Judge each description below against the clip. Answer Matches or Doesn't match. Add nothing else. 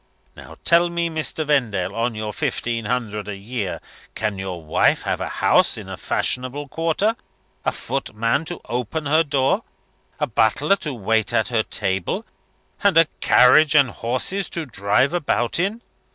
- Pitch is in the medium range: Doesn't match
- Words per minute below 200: Matches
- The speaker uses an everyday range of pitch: Doesn't match